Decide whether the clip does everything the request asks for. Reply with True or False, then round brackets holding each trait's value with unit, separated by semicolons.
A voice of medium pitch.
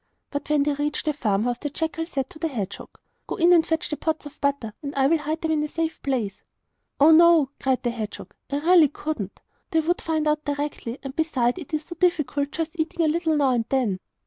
False (295 Hz)